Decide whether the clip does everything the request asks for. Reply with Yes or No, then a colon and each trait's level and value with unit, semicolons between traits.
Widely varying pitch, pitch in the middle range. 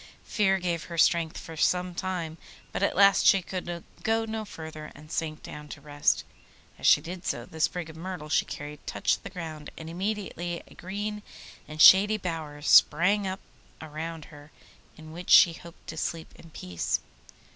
No: average, 3.2 semitones; medium, 170 Hz